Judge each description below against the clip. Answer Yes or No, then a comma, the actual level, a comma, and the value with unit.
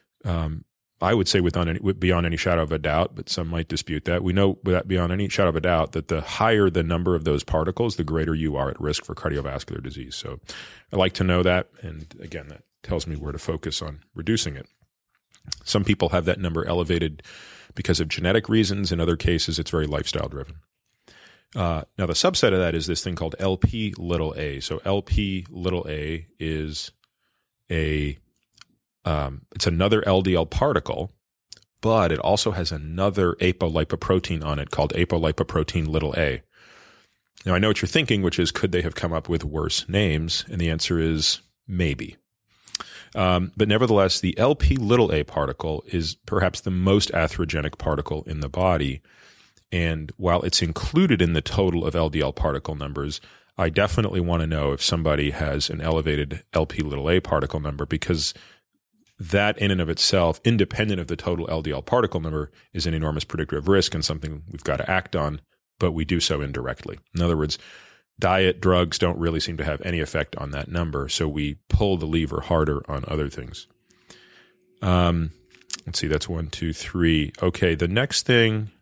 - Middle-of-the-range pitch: No, very low, 85 Hz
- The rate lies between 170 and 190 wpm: Yes, average, 185 wpm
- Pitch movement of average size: Yes, average, 3.0 semitones